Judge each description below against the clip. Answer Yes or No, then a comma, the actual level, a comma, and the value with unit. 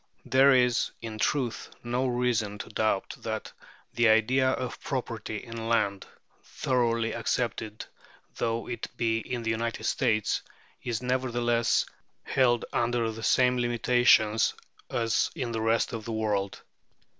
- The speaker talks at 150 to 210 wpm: No, slow, 135 wpm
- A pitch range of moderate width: No, narrow, 1.8 semitones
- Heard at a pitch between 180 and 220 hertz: No, low, 115 Hz